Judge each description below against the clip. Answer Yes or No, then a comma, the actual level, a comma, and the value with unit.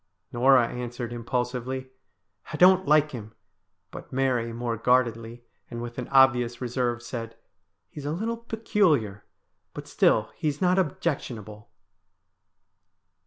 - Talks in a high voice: No, low, 125 Hz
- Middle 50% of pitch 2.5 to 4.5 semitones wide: Yes, average, 3.5 semitones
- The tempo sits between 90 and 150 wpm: Yes, average, 140 wpm